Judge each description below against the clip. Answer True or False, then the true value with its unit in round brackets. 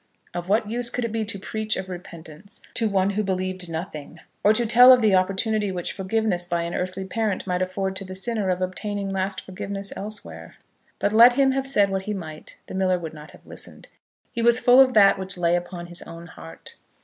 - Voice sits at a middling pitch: False (195 Hz)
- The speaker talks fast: True (220 wpm)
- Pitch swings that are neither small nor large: True (3.2 semitones)